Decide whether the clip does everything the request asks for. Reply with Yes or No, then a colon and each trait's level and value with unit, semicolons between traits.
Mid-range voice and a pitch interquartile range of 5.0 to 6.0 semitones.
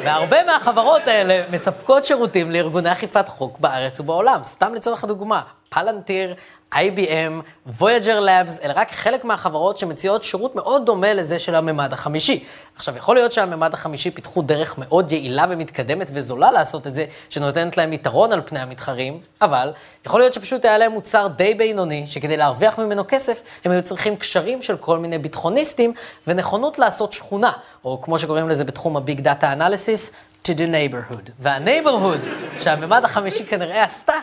Yes: medium, 180 Hz; wide, 5.6 semitones